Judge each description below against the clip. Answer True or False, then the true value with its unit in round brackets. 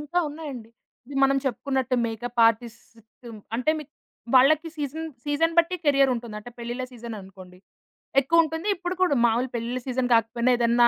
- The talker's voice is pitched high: True (255 Hz)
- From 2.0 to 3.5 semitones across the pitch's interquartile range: False (4.0 semitones)